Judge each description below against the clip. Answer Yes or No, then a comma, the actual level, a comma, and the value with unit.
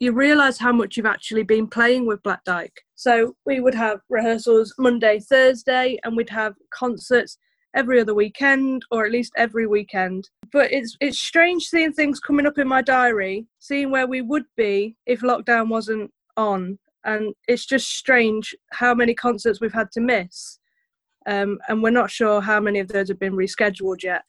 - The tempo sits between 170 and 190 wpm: Yes, average, 185 wpm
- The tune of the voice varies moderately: Yes, average, 3.6 semitones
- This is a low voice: No, high, 235 Hz